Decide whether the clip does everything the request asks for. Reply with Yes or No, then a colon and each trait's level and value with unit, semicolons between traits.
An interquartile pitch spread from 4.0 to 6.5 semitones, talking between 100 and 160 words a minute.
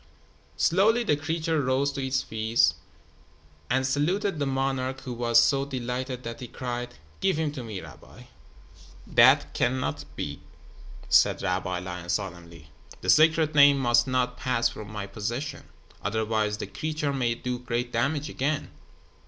No: average, 3.6 semitones; average, 145 wpm